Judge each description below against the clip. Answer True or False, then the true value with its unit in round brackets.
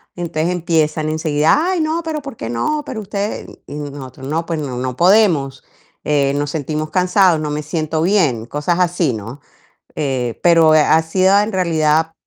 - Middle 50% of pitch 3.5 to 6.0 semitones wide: True (3.8 semitones)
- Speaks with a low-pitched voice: False (160 Hz)